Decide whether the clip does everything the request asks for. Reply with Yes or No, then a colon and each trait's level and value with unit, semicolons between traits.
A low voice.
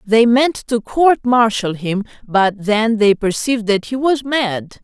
No: high, 225 Hz